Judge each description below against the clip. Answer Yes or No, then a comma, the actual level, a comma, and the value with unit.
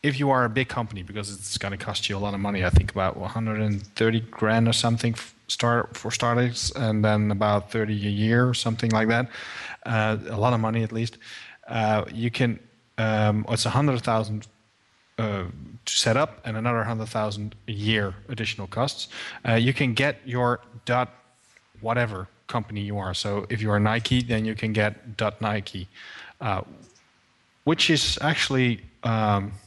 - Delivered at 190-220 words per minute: No, average, 180 wpm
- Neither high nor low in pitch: No, low, 110 Hz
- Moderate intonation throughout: No, narrow, 2.3 semitones